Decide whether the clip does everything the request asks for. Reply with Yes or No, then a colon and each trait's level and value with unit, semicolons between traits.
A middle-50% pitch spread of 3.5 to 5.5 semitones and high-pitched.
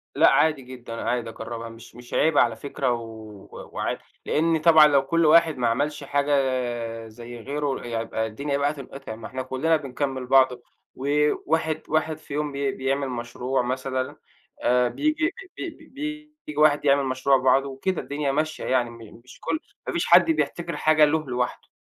No: average, 3.8 semitones; low, 135 Hz